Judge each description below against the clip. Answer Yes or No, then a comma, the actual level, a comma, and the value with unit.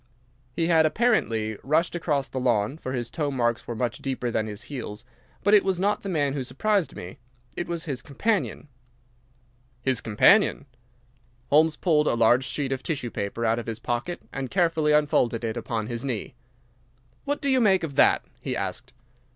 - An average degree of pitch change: No, wide, 5.9 semitones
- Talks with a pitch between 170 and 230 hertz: No, low, 135 Hz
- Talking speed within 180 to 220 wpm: Yes, average, 185 wpm